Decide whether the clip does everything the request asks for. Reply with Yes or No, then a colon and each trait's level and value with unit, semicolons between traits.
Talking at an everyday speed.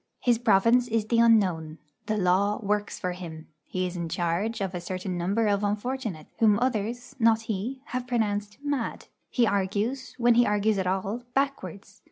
Yes: average, 175 wpm